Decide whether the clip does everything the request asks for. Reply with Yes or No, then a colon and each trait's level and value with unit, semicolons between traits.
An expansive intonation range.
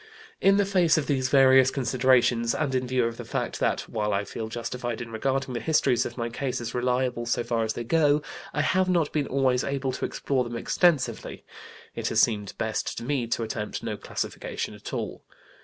No: average, 2.8 semitones